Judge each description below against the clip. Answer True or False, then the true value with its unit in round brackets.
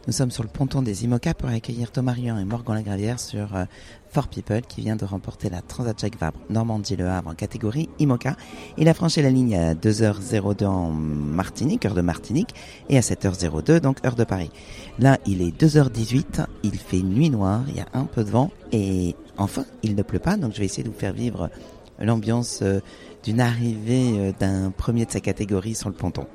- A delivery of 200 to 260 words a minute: True (210 wpm)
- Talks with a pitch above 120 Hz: False (110 Hz)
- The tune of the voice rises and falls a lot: False (4.1 semitones)